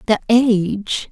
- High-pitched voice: Yes, high, 215 Hz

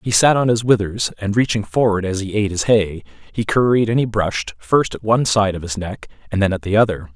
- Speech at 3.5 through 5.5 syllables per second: No, 5.9 syllables/s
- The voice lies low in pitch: Yes, low, 105 Hz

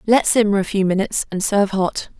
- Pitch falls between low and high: No, high, 200 Hz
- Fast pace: Yes, fast, 220 wpm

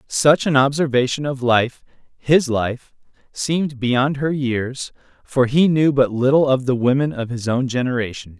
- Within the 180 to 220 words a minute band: No, average, 165 wpm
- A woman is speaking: No, male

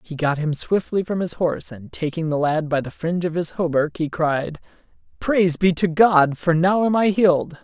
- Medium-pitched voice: Yes, medium, 170 Hz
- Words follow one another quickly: Yes, fast, 220 wpm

